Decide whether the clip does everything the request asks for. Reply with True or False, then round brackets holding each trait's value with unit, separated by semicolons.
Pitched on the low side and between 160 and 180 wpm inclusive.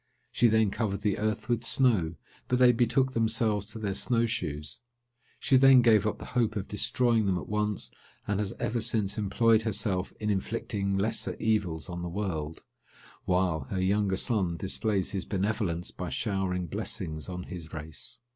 True (105 Hz; 170 wpm)